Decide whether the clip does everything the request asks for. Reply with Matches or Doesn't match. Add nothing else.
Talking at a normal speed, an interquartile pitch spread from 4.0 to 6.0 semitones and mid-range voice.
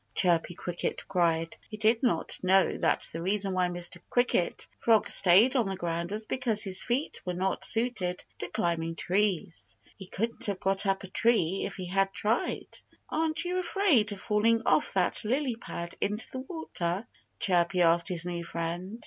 Doesn't match